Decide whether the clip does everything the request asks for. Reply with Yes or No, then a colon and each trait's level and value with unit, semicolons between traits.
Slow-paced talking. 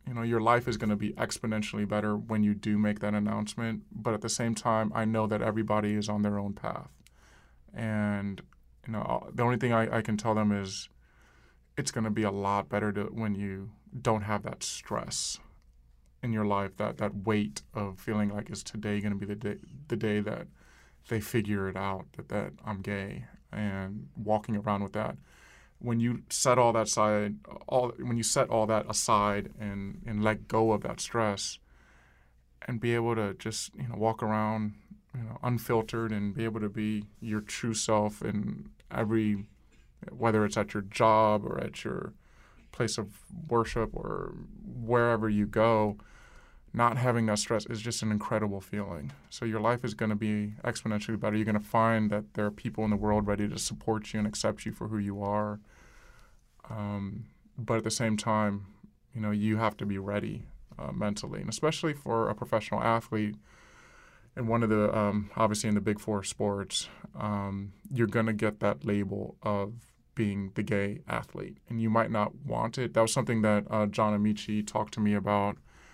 No: average, 195 wpm